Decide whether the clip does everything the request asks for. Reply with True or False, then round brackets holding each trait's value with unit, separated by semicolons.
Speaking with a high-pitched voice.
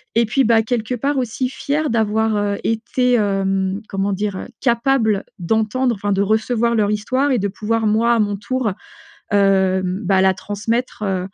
True (220 Hz)